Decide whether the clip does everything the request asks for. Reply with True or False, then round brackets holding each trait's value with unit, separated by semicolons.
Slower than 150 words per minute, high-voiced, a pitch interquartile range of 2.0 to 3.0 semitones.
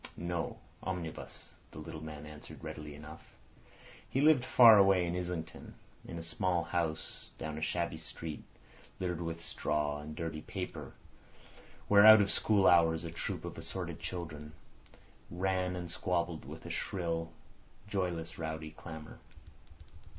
False (140 wpm; 85 Hz; 2.5 semitones)